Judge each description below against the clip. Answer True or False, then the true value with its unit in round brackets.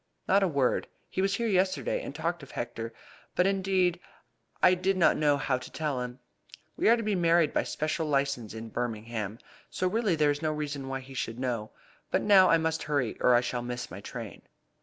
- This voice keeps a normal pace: False (210 wpm)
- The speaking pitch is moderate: True (150 Hz)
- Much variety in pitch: True (6.8 semitones)